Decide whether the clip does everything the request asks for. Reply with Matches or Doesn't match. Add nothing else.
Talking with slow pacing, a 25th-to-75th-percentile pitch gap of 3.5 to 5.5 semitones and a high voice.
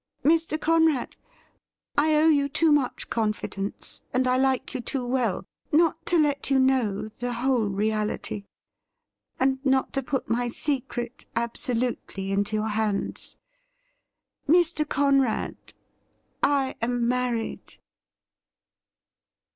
Matches